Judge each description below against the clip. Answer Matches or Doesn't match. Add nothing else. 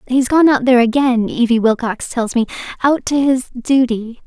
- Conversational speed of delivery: Matches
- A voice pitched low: Doesn't match